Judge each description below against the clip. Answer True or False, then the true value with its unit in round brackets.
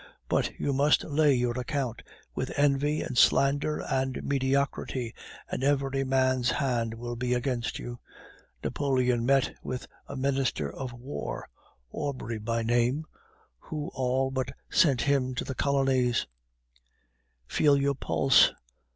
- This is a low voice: True (130 Hz)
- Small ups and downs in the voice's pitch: True (2.2 semitones)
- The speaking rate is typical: False (130 wpm)